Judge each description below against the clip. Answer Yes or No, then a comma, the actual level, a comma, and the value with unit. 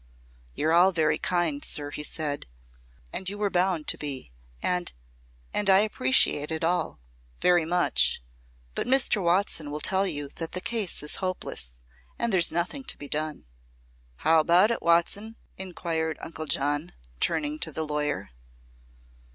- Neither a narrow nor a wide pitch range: Yes, average, 4.0 semitones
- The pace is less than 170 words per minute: Yes, average, 150 wpm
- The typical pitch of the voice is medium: Yes, medium, 170 Hz